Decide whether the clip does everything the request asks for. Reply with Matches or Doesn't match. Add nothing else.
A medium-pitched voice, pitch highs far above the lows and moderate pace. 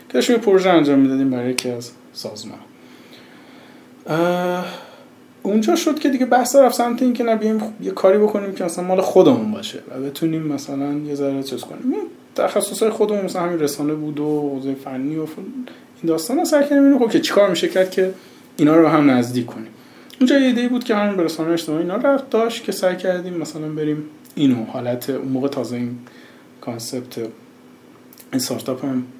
Doesn't match